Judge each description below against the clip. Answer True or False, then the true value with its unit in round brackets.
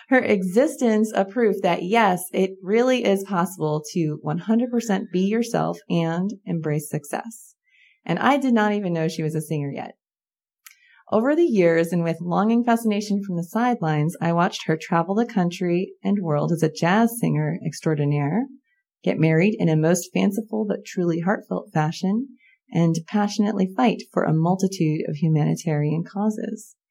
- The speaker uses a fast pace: False (155 wpm)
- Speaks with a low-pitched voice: False (190 Hz)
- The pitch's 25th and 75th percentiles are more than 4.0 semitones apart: True (5.3 semitones)